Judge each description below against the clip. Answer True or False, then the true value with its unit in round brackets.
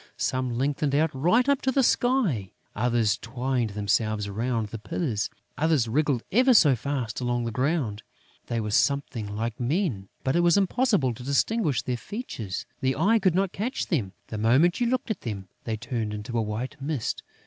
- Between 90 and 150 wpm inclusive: False (180 wpm)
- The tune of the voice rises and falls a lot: True (7.4 semitones)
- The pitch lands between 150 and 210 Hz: False (130 Hz)